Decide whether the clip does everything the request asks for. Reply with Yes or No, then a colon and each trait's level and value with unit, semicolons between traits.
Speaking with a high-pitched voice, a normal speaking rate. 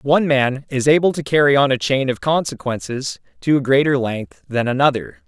No: low, 135 Hz; average, 195 wpm